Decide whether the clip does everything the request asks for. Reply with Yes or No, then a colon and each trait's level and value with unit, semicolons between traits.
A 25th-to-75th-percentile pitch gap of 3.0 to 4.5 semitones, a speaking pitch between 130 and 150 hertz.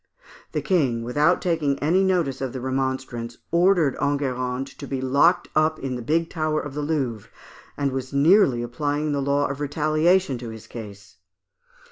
Yes: average, 3.4 semitones; medium, 140 Hz